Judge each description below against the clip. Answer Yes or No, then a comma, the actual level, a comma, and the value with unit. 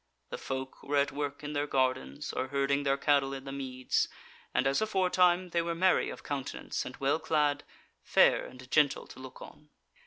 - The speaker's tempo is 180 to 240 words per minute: Yes, average, 190 wpm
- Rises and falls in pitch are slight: Yes, narrow, 2.1 semitones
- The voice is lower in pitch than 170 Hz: Yes, medium, 140 Hz